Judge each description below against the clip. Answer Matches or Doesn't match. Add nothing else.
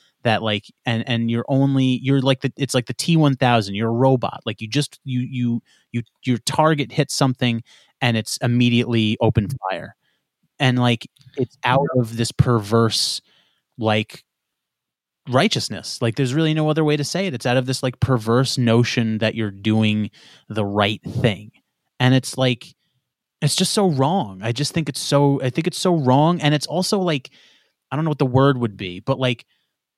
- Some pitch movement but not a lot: Matches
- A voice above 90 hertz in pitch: Matches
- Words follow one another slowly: Doesn't match